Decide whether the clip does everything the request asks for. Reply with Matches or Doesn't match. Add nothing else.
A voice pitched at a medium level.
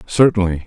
Doesn't match